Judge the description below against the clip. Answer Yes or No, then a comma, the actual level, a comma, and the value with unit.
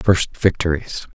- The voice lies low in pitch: Yes, very low, 85 Hz